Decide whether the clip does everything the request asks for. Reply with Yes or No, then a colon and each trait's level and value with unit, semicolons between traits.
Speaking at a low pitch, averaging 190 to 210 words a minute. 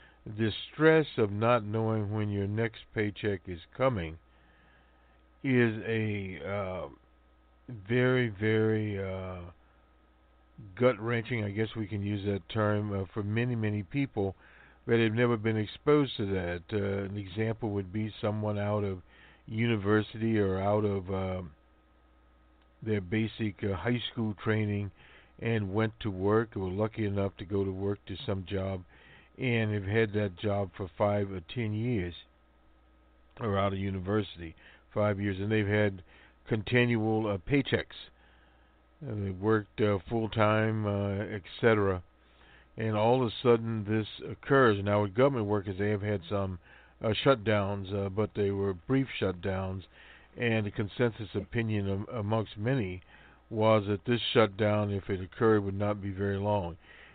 No: low, 105 Hz; average, 150 wpm